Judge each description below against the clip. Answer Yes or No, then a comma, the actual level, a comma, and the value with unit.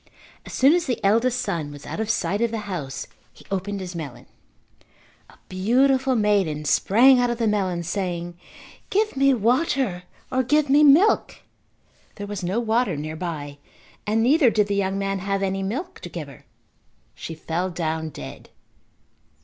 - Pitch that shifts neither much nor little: No, wide, 6.0 semitones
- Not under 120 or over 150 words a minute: No, average, 165 wpm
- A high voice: Yes, high, 205 Hz